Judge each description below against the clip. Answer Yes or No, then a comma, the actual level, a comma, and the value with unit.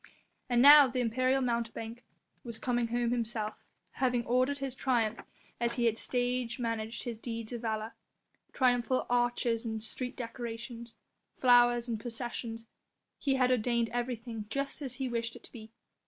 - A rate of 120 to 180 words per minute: Yes, average, 155 wpm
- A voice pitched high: Yes, high, 240 Hz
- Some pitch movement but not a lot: No, narrow, 1.7 semitones